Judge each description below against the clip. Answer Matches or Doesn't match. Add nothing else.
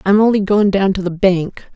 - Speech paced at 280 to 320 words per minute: Doesn't match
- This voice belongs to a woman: Matches